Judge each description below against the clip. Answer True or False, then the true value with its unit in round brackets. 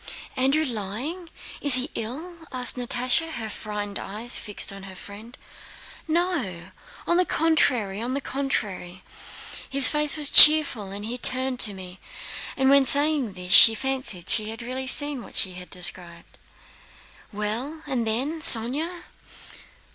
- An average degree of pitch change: False (5.7 semitones)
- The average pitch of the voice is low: False (250 Hz)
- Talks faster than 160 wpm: False (145 wpm)